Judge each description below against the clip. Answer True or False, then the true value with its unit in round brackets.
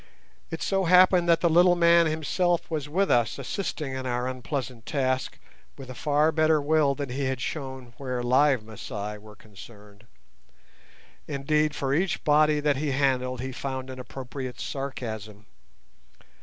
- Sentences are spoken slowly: False (155 wpm)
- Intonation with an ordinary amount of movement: True (3.6 semitones)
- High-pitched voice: False (135 Hz)